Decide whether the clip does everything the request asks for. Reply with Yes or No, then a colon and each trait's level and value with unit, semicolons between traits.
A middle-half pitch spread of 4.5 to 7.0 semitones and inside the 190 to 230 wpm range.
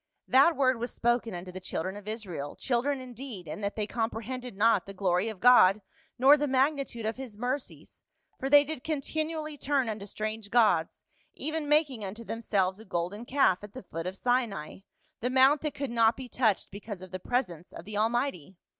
Yes: average, 5.1 semitones; average, 195 wpm